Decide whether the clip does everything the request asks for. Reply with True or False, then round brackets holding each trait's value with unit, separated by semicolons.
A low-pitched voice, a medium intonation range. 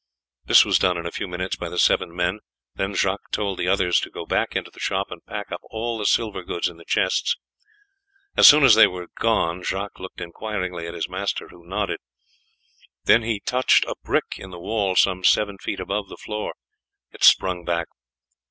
True (95 Hz; 3.0 semitones)